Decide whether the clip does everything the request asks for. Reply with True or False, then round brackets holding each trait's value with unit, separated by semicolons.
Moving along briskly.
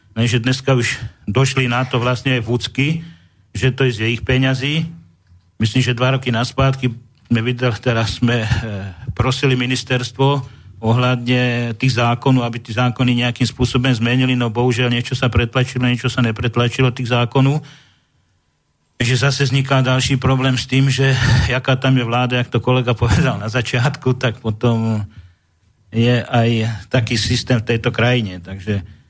False (150 wpm)